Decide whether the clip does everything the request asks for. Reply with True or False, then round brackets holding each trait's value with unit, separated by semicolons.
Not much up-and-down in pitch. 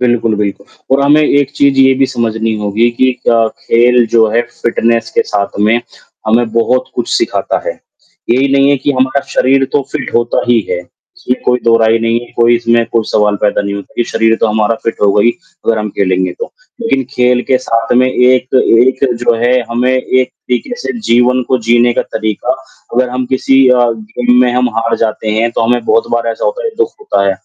True (2.2 semitones)